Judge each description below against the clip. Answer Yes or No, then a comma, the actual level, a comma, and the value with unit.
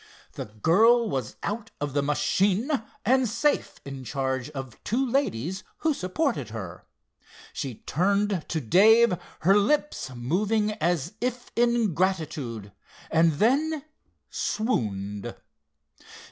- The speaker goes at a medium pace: No, slow, 115 wpm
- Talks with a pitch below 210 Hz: Yes, medium, 185 Hz